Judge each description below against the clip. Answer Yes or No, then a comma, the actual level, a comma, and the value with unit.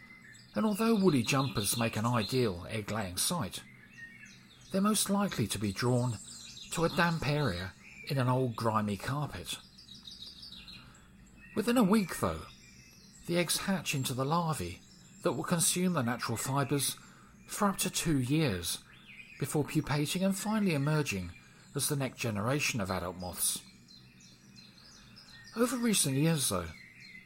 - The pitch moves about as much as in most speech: No, wide, 8.5 semitones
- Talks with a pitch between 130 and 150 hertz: Yes, low, 135 Hz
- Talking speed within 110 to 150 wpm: Yes, slow, 135 wpm